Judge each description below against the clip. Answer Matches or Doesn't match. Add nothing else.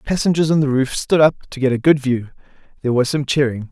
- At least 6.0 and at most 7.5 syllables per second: Matches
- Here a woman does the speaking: Doesn't match